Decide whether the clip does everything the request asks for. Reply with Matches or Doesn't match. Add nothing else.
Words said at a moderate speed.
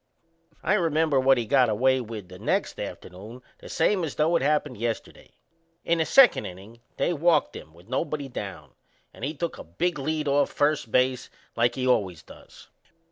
Matches